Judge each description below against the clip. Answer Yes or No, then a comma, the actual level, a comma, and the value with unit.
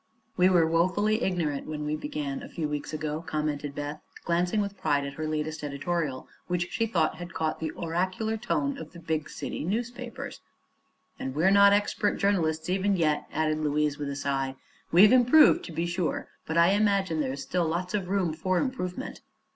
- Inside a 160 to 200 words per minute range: Yes, average, 185 wpm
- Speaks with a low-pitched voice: No, medium, 170 Hz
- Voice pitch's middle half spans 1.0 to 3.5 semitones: No, average, 4.1 semitones